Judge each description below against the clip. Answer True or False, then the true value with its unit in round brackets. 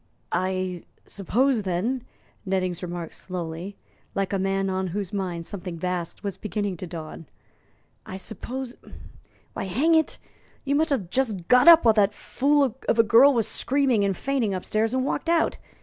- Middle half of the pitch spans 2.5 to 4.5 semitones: False (5.5 semitones)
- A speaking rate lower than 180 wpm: True (165 wpm)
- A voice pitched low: False (200 Hz)